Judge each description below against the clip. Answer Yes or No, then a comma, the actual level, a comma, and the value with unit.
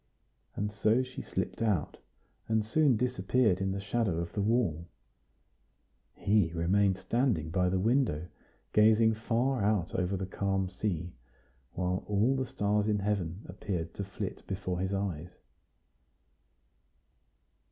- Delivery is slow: Yes, slow, 130 wpm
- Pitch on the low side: Yes, low, 100 Hz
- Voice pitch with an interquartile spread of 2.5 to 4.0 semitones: Yes, average, 3.4 semitones